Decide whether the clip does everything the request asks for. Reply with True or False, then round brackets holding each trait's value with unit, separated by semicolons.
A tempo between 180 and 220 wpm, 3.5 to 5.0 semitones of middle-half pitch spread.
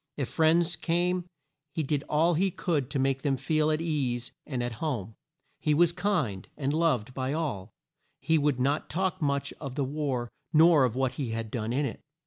True (195 wpm; 4.0 semitones)